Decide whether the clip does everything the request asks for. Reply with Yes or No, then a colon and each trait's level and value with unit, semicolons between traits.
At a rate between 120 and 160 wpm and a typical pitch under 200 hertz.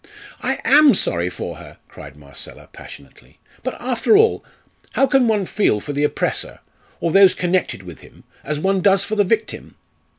No: average, 170 wpm; high, 190 Hz